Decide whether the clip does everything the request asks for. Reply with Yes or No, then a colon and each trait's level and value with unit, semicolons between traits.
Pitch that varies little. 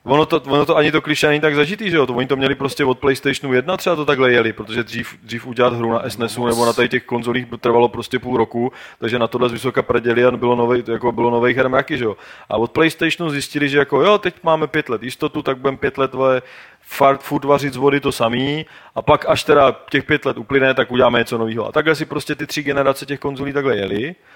No: average, 3.4 semitones